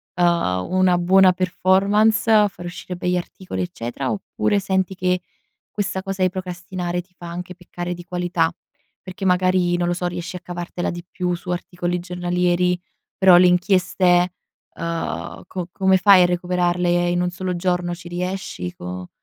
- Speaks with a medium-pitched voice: Yes, medium, 180 Hz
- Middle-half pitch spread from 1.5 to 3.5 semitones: No, narrow, 1.0 semitones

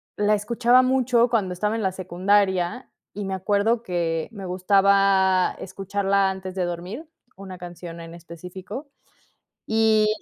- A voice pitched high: Yes, high, 195 Hz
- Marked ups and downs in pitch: No, average, 2.9 semitones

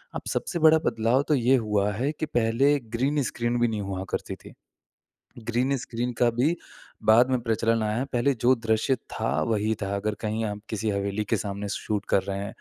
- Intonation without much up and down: No, average, 3.2 semitones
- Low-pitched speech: Yes, low, 115 Hz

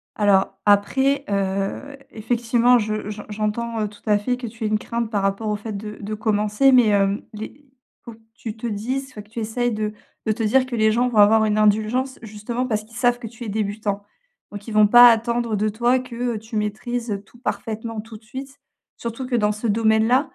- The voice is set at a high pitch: Yes, high, 220 Hz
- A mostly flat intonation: Yes, narrow, 2.3 semitones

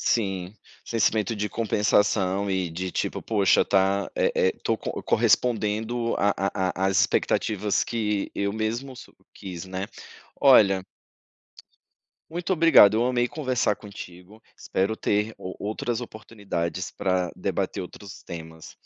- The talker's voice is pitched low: Yes, low, 105 Hz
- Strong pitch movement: No, average, 3.0 semitones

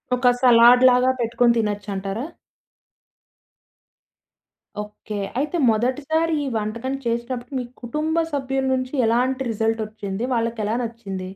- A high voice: Yes, high, 235 Hz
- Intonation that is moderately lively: Yes, average, 3.0 semitones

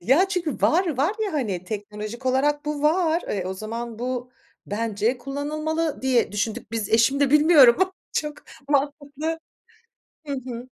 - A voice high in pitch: Yes, very high, 265 Hz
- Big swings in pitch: No, average, 4.7 semitones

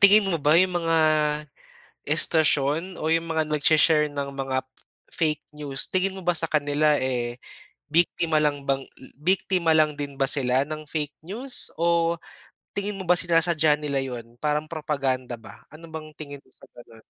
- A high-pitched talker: No, medium, 155 Hz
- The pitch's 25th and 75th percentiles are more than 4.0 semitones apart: No, average, 3.1 semitones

